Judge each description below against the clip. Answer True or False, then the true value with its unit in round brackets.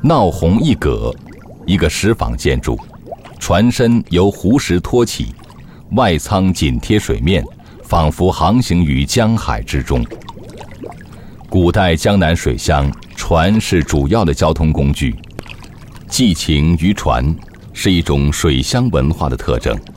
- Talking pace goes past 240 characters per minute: False (185 characters per minute)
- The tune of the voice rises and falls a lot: False (4.8 semitones)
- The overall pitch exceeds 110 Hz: False (85 Hz)